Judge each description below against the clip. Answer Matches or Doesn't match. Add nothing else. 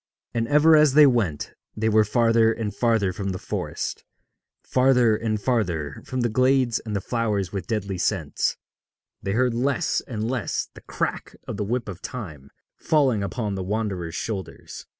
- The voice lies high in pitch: Doesn't match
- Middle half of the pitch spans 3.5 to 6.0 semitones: Matches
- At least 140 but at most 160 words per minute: Doesn't match